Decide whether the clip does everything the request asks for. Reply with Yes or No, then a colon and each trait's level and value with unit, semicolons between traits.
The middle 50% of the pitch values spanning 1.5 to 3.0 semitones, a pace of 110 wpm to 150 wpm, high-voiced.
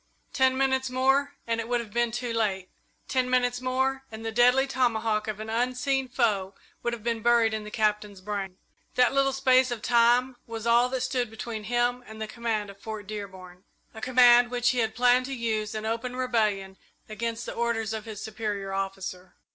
No: average, 2.7 semitones; average, 195 wpm; high, 235 Hz